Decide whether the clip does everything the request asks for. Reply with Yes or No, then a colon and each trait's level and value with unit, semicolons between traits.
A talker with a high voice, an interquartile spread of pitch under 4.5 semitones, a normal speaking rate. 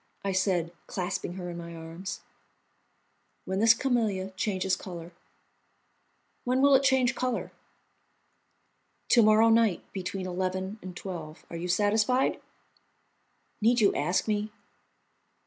No: high, 195 Hz; average, 3.9 semitones; slow, 120 wpm